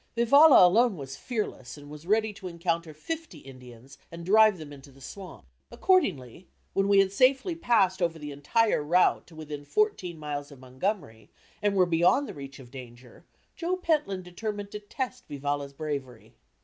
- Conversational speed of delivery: Yes, average, 170 wpm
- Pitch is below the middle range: No, medium, 175 Hz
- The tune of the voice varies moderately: No, wide, 7.0 semitones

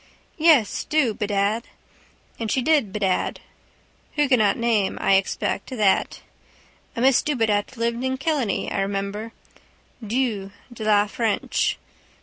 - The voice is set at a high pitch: Yes, high, 225 Hz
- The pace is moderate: No, slow, 125 wpm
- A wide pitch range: No, average, 4.1 semitones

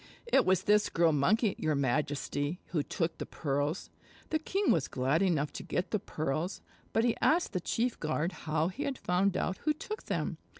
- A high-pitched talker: No, medium, 175 Hz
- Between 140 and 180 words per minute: No, average, 195 wpm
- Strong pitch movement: Yes, wide, 6.3 semitones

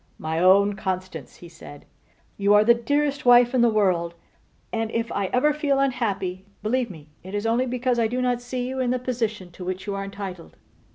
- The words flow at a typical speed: No, fast, 210 wpm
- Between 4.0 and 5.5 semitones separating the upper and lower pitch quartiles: Yes, average, 4.8 semitones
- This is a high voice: Yes, high, 220 Hz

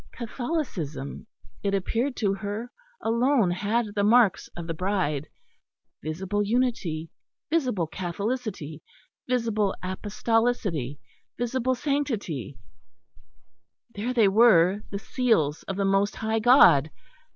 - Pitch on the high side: Yes, high, 205 Hz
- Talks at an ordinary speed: No, slow, 105 wpm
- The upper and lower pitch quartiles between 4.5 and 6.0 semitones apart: Yes, average, 5.1 semitones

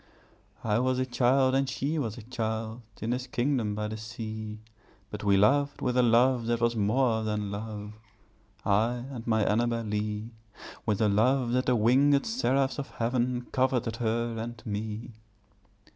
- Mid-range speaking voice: No, low, 115 Hz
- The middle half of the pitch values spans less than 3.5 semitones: Yes, average, 2.7 semitones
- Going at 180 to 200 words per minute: No, average, 165 wpm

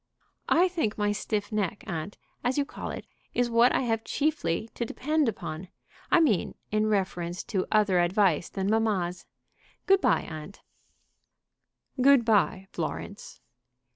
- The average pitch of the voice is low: No, high, 215 Hz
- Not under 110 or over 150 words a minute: Yes, average, 140 wpm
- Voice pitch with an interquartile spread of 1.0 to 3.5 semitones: No, average, 4.3 semitones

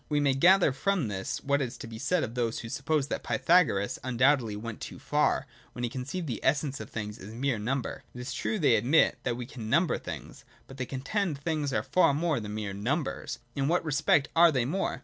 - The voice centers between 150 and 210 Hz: No, low, 135 Hz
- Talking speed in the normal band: No, fast, 230 wpm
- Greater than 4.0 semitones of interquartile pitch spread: Yes, average, 4.6 semitones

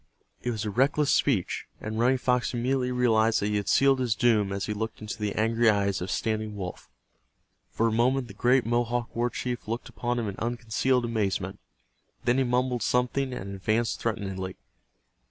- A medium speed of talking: Yes, average, 185 wpm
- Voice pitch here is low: Yes, low, 115 Hz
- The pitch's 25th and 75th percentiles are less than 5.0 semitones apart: Yes, average, 2.8 semitones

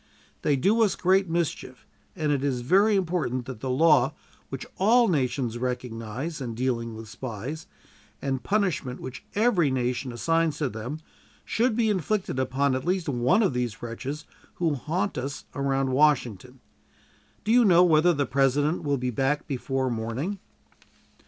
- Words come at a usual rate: Yes, average, 160 wpm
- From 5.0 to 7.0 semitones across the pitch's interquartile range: Yes, average, 5.3 semitones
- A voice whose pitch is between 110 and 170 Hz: Yes, medium, 140 Hz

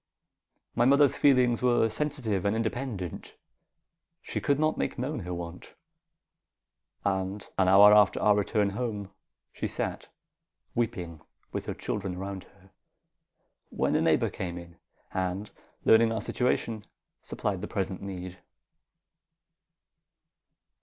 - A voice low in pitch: Yes, low, 105 Hz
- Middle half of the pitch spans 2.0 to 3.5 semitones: No, average, 4.2 semitones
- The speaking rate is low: Yes, slow, 120 wpm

